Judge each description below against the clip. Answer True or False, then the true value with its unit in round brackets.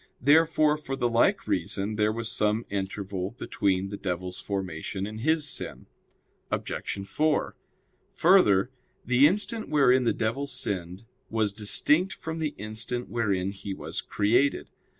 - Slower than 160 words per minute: True (135 wpm)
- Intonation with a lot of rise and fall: True (6.3 semitones)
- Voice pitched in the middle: False (110 Hz)